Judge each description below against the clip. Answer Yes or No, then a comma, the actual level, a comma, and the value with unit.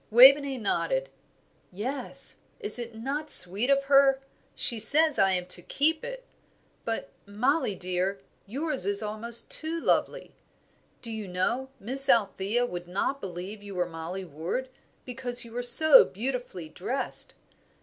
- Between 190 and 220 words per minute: No, average, 140 wpm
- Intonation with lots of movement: Yes, wide, 6.1 semitones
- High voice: Yes, high, 230 Hz